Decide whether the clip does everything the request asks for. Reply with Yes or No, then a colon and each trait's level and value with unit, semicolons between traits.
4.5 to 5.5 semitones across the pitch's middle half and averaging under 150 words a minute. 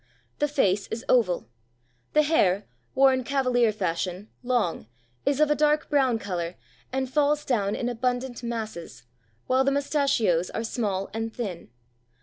Yes: average, 5.2 semitones; average, 140 wpm